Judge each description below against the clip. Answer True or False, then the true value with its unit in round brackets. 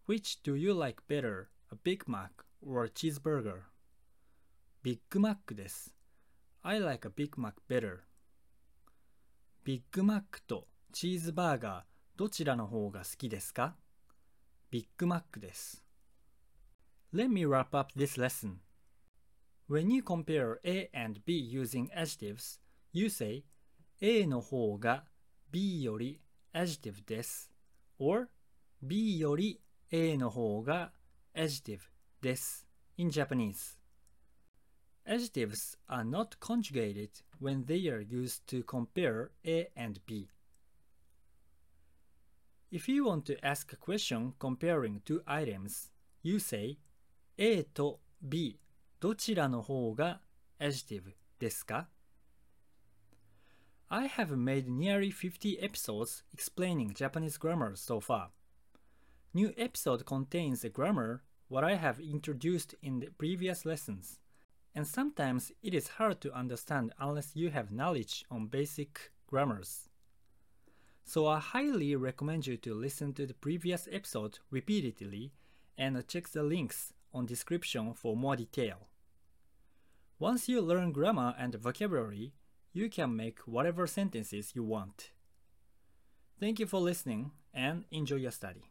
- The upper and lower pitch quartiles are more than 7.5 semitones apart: True (8.3 semitones)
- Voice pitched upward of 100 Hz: True (135 Hz)